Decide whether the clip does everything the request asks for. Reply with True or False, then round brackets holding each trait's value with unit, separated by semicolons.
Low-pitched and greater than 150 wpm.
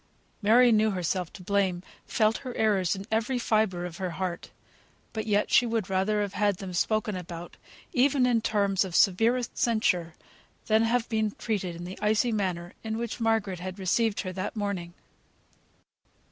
False (205 Hz; 170 wpm)